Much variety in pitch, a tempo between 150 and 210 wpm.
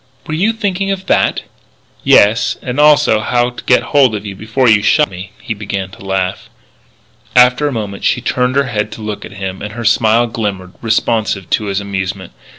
No: average, 4.0 semitones; average, 195 wpm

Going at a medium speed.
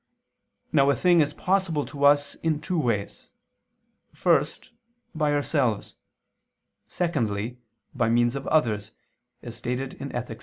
No: slow, 125 wpm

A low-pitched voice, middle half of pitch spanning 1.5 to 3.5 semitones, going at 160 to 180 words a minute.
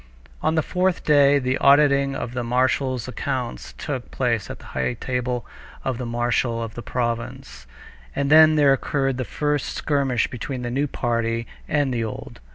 Yes: low, 130 Hz; average, 2.9 semitones; average, 170 wpm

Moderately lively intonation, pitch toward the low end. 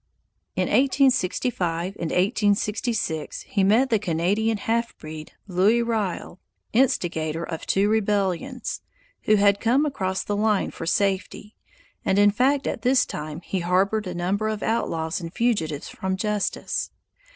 No: average, 4.1 semitones; high, 205 Hz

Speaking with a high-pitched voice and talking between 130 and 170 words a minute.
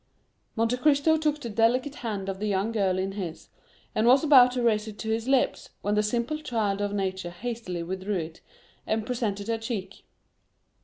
No: high, 220 Hz; average, 190 wpm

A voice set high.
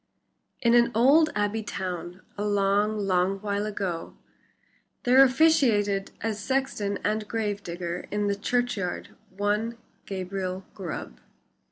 Yes: high, 205 Hz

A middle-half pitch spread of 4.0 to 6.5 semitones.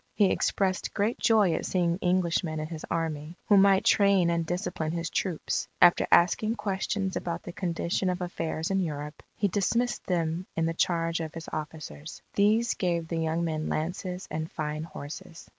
No: average, 2.9 semitones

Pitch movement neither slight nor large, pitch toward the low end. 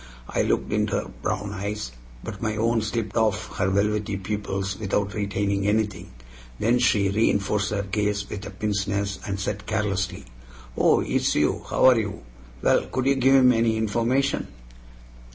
No: narrow, 2.0 semitones; low, 105 Hz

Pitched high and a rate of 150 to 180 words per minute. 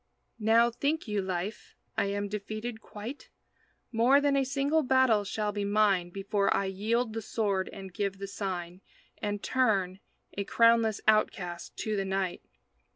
Yes: high, 210 Hz; average, 155 wpm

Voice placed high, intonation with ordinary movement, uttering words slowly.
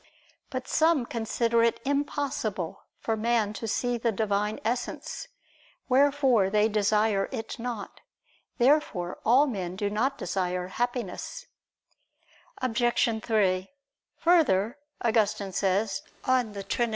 Yes: high, 225 Hz; average, 3.6 semitones; slow, 110 wpm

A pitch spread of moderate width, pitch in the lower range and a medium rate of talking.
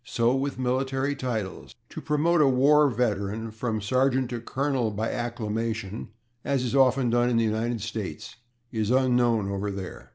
Yes: average, 3.2 semitones; low, 120 Hz; average, 160 wpm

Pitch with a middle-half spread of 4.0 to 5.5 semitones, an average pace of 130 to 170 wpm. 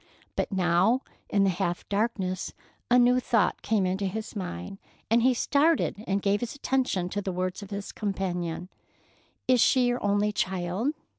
Yes: average, 4.4 semitones; average, 165 wpm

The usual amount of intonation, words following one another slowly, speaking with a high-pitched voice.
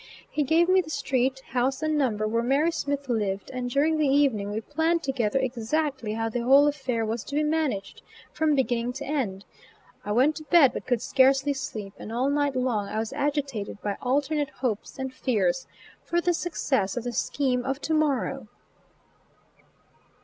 No: average, 4.1 semitones; average, 180 wpm; very high, 265 Hz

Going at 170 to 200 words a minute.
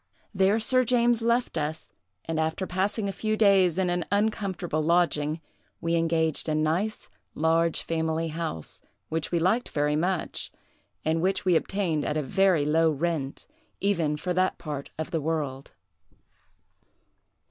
No: average, 145 wpm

